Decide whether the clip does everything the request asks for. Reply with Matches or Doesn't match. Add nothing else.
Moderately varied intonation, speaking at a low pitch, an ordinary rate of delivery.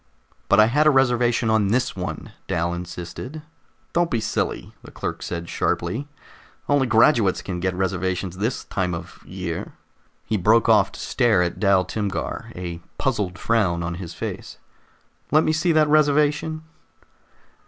Doesn't match